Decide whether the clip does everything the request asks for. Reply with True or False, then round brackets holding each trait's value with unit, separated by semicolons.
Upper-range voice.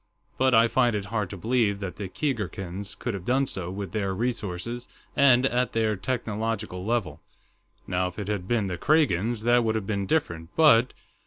False (110 Hz)